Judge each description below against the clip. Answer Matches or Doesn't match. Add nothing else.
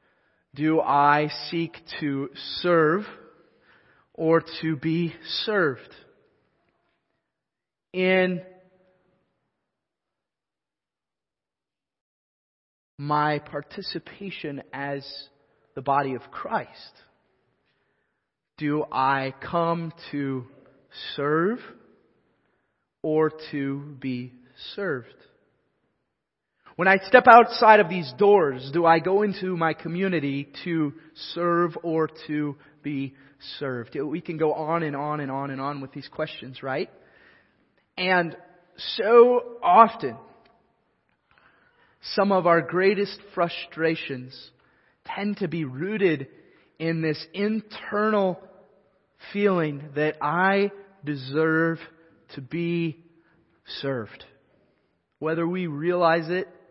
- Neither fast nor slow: Doesn't match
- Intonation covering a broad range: Doesn't match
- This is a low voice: Doesn't match